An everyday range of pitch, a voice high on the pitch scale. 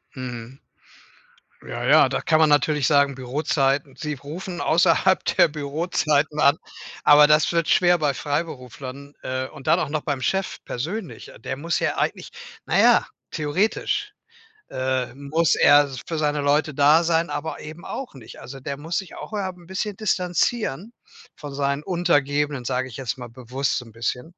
No: average, 3.6 semitones; medium, 145 Hz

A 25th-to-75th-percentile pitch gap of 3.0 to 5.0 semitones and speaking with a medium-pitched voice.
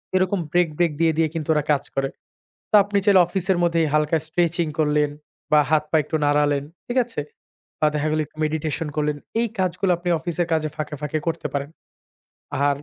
No: narrow, 2.6 semitones; medium, 160 Hz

